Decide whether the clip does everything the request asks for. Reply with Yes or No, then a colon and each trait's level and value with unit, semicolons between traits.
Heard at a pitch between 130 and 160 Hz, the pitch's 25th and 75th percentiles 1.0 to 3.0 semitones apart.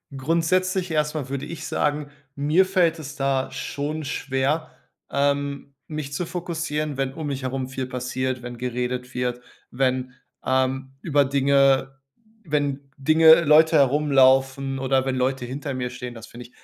Yes: low, 135 Hz; narrow, 2.6 semitones